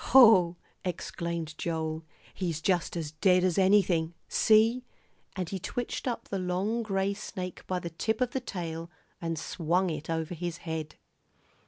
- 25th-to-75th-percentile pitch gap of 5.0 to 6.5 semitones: No, average, 3.2 semitones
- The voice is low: No, medium, 180 Hz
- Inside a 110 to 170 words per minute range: Yes, average, 155 wpm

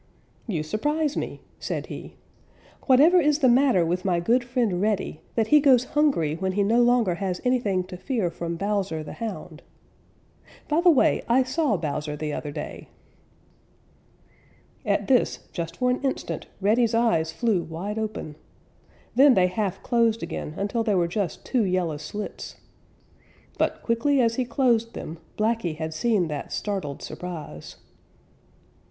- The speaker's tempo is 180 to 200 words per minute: No, average, 155 wpm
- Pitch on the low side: No, high, 210 Hz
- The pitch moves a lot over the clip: Yes, wide, 6.2 semitones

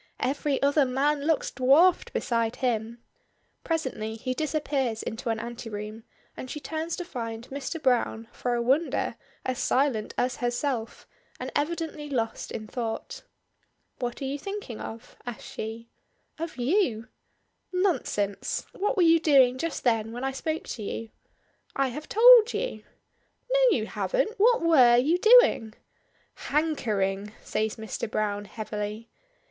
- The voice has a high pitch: Yes, very high, 255 Hz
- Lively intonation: Yes, wide, 5.8 semitones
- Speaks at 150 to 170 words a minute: No, average, 140 wpm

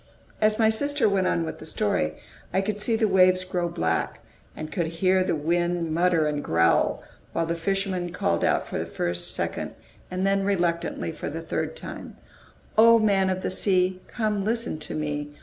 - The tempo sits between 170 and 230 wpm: Yes, average, 185 wpm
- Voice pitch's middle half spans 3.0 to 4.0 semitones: Yes, average, 3.6 semitones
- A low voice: No, medium, 185 Hz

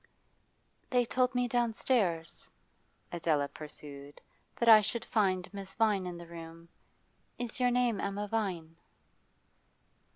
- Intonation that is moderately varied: No, wide, 5.8 semitones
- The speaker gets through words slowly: Yes, slow, 120 wpm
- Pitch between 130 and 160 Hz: No, high, 200 Hz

